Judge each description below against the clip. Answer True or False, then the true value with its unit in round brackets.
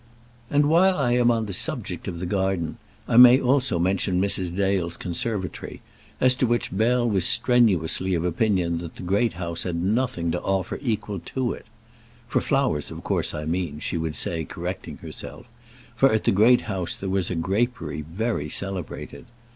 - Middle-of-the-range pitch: False (95 Hz)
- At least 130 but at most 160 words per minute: False (180 wpm)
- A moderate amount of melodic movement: False (5.7 semitones)